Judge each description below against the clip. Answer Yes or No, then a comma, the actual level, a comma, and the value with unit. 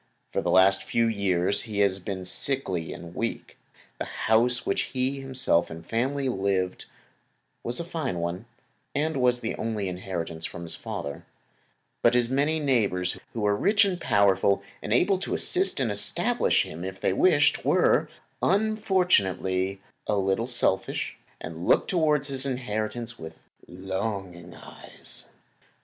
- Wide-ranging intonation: Yes, wide, 6.0 semitones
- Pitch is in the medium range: No, low, 110 Hz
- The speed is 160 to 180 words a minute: No, average, 145 wpm